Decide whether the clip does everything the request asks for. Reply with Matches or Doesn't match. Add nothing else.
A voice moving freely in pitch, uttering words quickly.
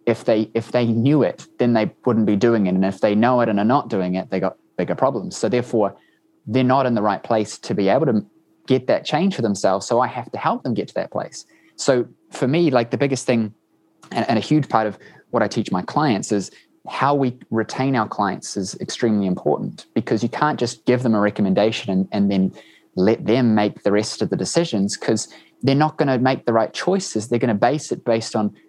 Doesn't match